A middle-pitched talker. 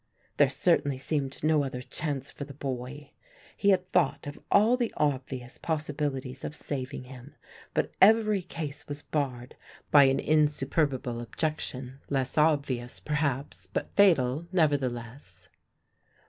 Yes: medium, 145 Hz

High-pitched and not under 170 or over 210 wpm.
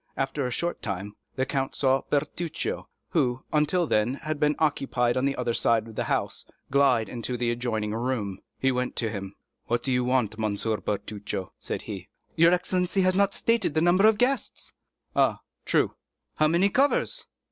No: low, 130 Hz; average, 180 wpm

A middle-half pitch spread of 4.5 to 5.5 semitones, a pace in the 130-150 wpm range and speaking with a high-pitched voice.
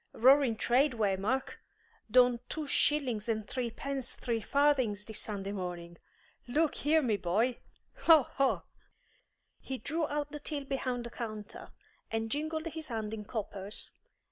Yes: average, 4.9 semitones; average, 140 wpm; high, 245 Hz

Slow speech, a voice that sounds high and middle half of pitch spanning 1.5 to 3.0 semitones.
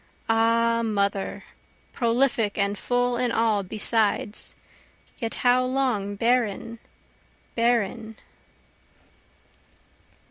Yes: slow, 75 wpm; high, 230 Hz; average, 2.7 semitones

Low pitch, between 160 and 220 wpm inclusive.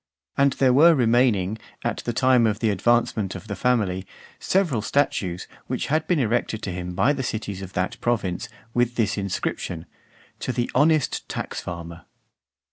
Yes: low, 115 Hz; average, 165 wpm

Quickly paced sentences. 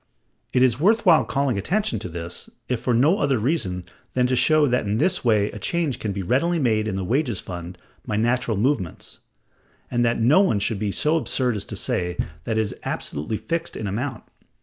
Yes: fast, 210 wpm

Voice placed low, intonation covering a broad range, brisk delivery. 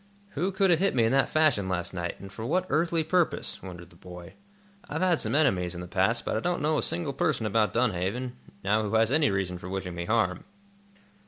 Yes: low, 110 Hz; wide, 8.9 semitones; fast, 230 wpm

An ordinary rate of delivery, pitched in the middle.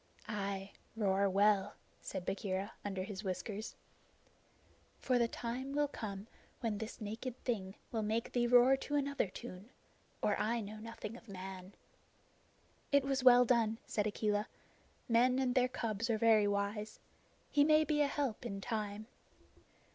No: average, 150 wpm; high, 220 Hz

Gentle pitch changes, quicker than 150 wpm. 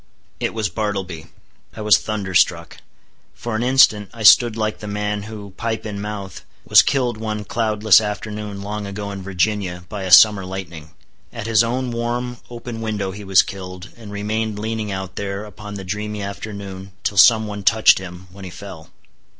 Yes: narrow, 2.1 semitones; average, 175 wpm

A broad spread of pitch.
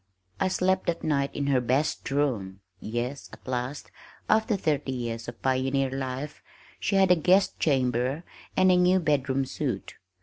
No: average, 4.7 semitones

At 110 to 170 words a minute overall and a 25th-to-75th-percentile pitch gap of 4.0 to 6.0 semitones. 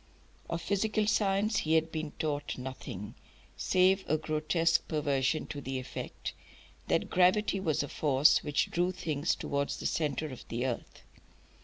Yes: average, 150 wpm; average, 4.3 semitones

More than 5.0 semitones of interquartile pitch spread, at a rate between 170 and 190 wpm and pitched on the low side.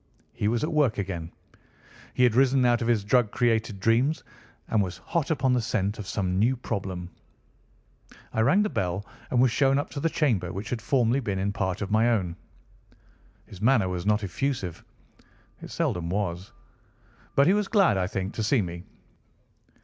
Yes: wide, 5.4 semitones; average, 180 wpm; low, 110 Hz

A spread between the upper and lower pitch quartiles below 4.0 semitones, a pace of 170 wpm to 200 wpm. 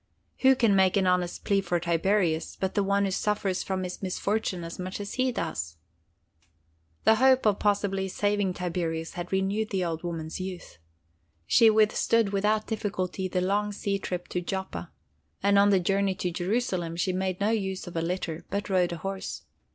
Yes: narrow, 2.4 semitones; average, 180 wpm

